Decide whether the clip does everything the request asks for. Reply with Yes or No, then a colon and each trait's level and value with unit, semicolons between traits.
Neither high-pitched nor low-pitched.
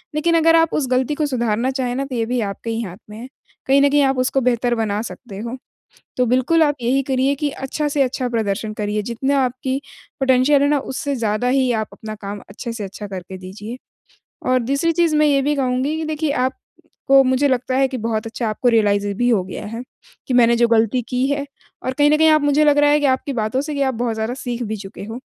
No: very high, 255 Hz